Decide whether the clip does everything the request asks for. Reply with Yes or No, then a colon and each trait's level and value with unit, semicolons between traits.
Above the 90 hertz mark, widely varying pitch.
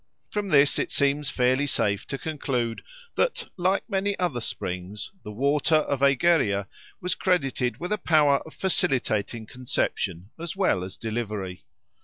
Yes: medium, 140 Hz; wide, 7.5 semitones